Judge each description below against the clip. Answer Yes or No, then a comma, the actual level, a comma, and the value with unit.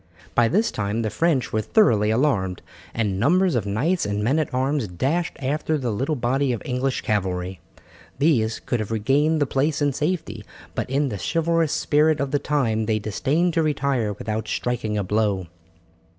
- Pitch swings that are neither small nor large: No, wide, 5.7 semitones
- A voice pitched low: Yes, low, 125 Hz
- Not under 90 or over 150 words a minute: No, average, 180 wpm